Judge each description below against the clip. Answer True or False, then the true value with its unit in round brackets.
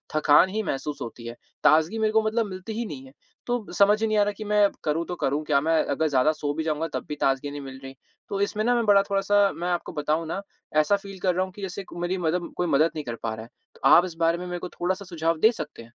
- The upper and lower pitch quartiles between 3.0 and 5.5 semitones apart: True (5.1 semitones)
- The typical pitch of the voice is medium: True (175 Hz)